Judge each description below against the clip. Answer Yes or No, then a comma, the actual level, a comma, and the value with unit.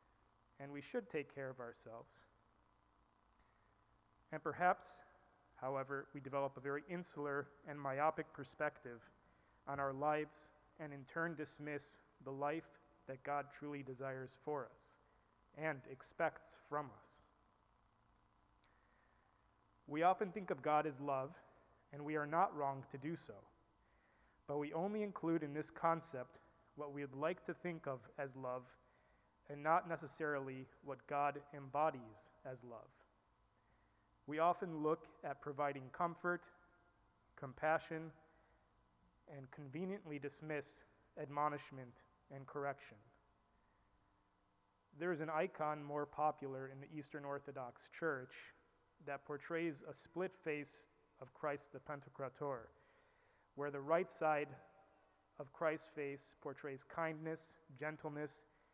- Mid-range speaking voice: Yes, medium, 145 Hz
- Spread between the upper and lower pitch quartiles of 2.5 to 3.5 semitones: Yes, average, 3.1 semitones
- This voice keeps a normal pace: No, slow, 120 wpm